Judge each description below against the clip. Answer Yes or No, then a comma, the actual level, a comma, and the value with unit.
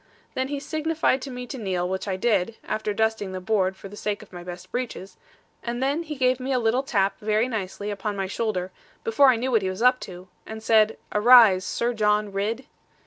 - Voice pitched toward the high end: Yes, high, 220 Hz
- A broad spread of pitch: No, average, 4.4 semitones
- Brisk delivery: Yes, fast, 220 wpm